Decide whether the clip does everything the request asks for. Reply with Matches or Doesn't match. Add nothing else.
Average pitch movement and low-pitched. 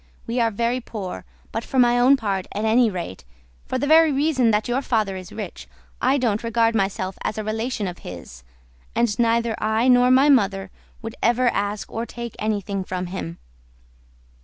Doesn't match